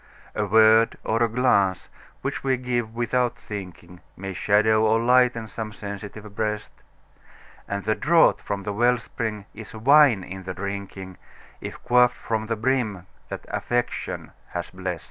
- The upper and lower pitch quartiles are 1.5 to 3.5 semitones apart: Yes, average, 3.2 semitones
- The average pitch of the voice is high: No, low, 110 Hz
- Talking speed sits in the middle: Yes, average, 150 wpm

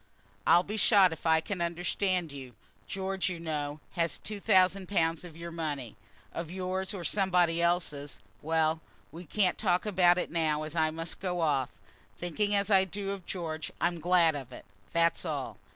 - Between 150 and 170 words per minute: No, average, 185 wpm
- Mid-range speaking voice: Yes, medium, 170 Hz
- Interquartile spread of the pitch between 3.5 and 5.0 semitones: No, average, 2.9 semitones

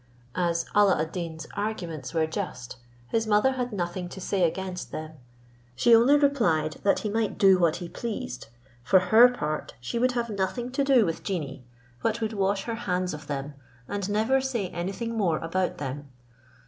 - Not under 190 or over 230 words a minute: No, average, 180 wpm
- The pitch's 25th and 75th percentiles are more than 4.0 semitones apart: Yes, wide, 5.6 semitones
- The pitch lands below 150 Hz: No, high, 190 Hz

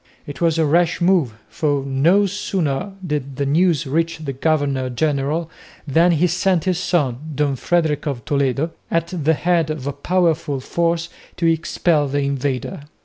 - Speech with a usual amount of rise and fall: Yes, average, 3.4 semitones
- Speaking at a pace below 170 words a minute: Yes, average, 160 wpm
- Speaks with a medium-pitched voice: Yes, medium, 155 Hz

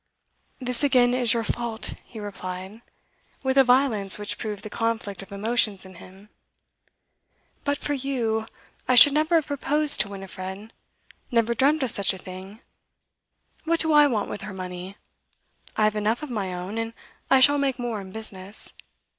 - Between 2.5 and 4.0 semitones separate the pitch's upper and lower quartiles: No, average, 4.8 semitones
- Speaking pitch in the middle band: No, high, 225 Hz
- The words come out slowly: No, average, 170 wpm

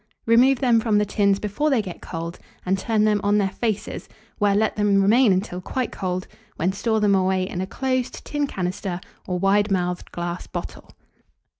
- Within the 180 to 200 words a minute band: Yes, average, 185 wpm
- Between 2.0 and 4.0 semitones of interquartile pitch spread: Yes, average, 3.0 semitones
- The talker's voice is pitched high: Yes, high, 200 Hz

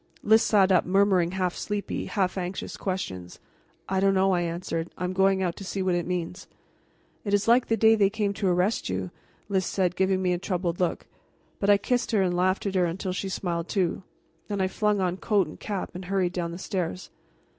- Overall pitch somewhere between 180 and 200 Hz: Yes, high, 190 Hz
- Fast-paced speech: Yes, fast, 220 wpm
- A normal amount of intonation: No, narrow, 1.9 semitones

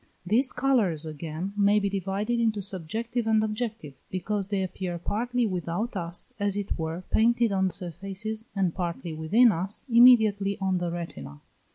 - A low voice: No, high, 200 Hz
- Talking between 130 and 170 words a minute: Yes, average, 155 wpm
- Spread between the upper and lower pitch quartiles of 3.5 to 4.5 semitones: Yes, average, 3.9 semitones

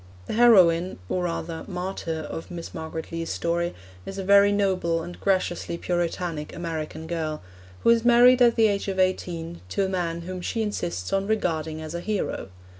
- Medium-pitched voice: Yes, medium, 175 Hz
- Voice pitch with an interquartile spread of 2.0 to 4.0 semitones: Yes, average, 3.1 semitones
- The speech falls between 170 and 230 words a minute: Yes, average, 180 wpm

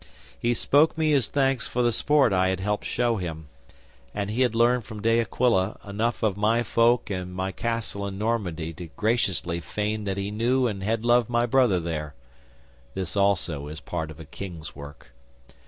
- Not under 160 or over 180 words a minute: No, average, 190 wpm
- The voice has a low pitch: Yes, low, 105 Hz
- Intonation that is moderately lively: Yes, average, 4.3 semitones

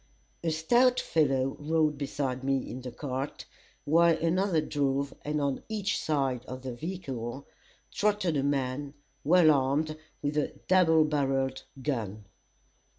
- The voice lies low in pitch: No, medium, 145 Hz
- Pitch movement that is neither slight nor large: Yes, average, 3.3 semitones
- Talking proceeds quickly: No, slow, 135 wpm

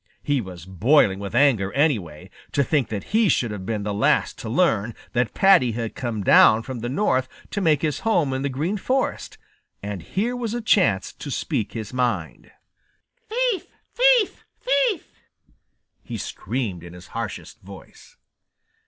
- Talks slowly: No, average, 160 wpm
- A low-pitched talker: Yes, low, 125 Hz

